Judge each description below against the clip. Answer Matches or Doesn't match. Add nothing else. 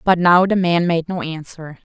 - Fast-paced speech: Matches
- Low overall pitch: Doesn't match